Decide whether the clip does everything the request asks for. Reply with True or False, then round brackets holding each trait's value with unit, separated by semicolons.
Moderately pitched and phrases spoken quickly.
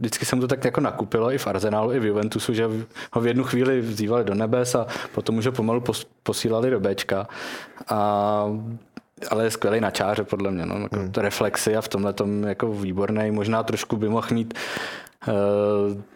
False (110 Hz; 200 wpm)